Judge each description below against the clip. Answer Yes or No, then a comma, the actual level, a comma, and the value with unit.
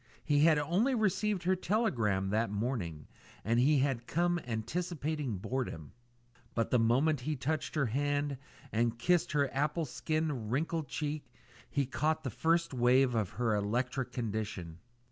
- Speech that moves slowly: No, average, 145 wpm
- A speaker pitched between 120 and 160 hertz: Yes, low, 135 Hz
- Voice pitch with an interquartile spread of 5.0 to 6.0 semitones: Yes, average, 5.3 semitones